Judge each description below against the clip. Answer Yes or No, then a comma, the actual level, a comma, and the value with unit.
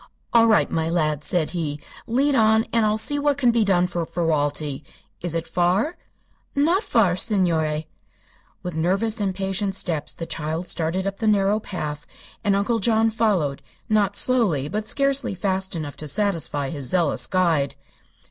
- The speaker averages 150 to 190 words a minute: Yes, average, 160 wpm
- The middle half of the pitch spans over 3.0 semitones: Yes, average, 5.3 semitones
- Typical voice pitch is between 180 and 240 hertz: Yes, high, 190 Hz